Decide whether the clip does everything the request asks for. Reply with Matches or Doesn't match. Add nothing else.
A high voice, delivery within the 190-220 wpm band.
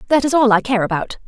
Doesn't match